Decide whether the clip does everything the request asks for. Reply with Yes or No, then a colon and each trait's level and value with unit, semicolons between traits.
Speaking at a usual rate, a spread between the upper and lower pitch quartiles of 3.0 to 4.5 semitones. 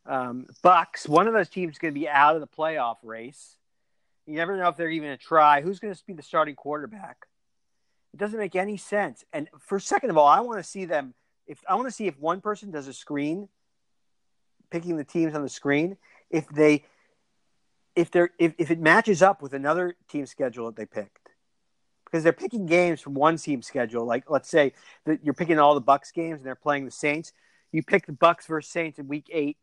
No: fast, 225 wpm; average, 3.8 semitones